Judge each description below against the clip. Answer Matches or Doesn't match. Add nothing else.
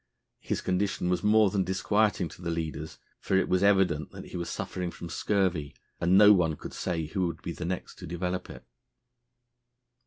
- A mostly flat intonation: Matches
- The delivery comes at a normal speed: Matches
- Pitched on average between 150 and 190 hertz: Doesn't match